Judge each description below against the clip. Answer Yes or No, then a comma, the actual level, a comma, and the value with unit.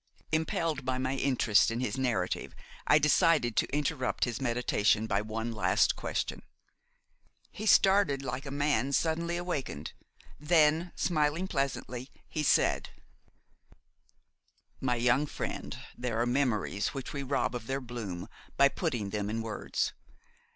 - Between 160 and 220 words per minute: No, slow, 135 wpm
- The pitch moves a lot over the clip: No, average, 4.2 semitones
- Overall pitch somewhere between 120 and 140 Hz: Yes, low, 135 Hz